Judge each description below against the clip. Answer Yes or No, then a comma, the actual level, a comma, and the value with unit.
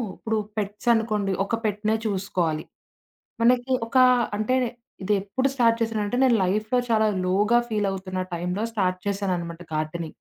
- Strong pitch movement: No, average, 3.3 semitones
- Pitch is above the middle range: Yes, high, 205 Hz